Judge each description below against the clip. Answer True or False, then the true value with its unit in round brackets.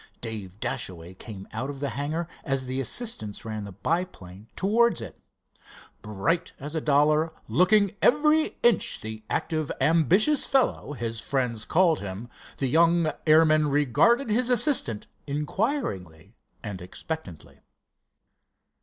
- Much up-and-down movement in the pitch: True (8.1 semitones)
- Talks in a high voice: False (145 Hz)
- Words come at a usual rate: False (125 wpm)